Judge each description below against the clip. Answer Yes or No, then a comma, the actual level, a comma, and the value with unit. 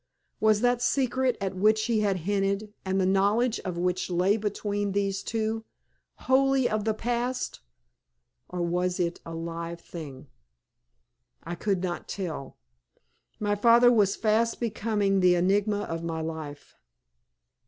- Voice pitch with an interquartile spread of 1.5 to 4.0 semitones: Yes, average, 3.6 semitones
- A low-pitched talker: No, high, 200 Hz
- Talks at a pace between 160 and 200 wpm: No, average, 140 wpm